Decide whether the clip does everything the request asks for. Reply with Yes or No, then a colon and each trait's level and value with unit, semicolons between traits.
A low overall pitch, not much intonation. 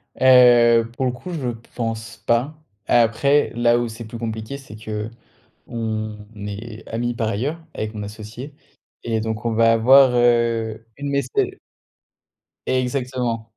Yes: low, 115 Hz; narrow, 2.1 semitones